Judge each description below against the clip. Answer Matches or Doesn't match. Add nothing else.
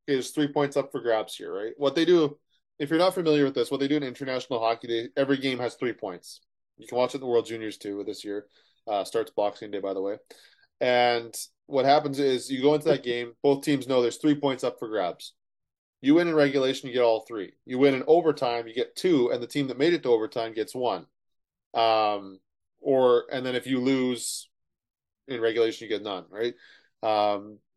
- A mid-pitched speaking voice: Doesn't match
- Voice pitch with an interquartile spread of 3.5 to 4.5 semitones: Matches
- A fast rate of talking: Matches